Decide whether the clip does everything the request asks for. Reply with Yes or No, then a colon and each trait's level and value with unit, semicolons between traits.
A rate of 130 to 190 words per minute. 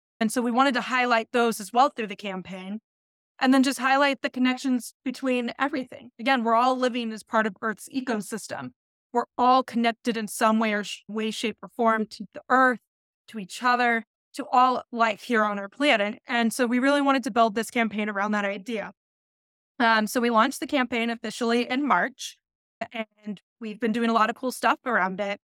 No: fast, 205 wpm